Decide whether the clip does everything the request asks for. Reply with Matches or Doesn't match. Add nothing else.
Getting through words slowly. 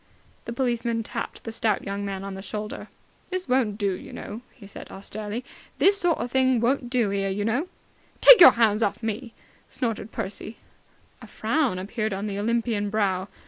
Doesn't match